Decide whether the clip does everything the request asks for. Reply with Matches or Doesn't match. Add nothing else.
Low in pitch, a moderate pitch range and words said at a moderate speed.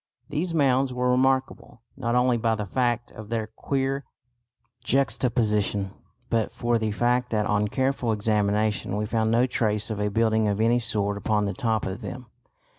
Matches